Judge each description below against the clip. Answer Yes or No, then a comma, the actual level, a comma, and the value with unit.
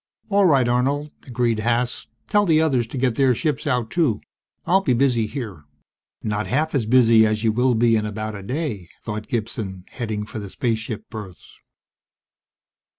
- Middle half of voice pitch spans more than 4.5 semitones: No, average, 3.7 semitones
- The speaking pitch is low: Yes, low, 120 Hz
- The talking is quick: No, average, 170 wpm